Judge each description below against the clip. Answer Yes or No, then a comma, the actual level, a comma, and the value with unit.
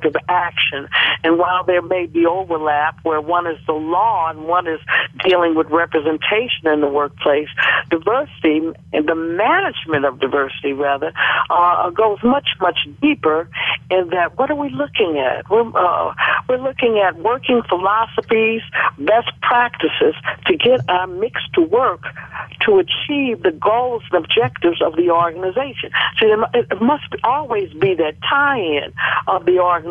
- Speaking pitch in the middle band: Yes, medium, 180 Hz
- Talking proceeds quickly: No, average, 150 wpm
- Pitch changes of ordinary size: No, wide, 6.8 semitones